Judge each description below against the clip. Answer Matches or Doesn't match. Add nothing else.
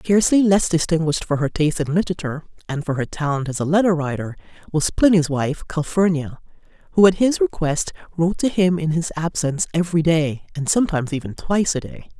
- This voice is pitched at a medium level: Matches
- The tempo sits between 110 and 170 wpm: Doesn't match